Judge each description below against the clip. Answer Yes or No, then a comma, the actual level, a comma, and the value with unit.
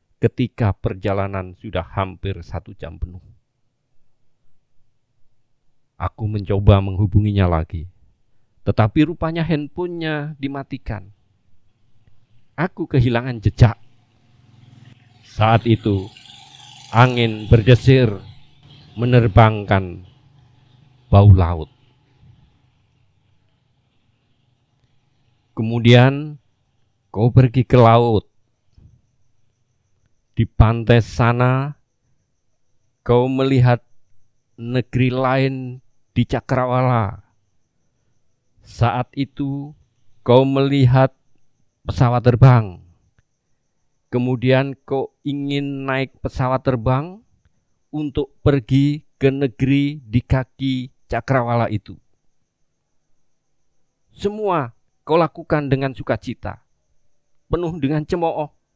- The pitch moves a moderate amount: Yes, average, 3.3 semitones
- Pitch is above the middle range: No, low, 120 Hz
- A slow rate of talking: Yes, slow, 70 wpm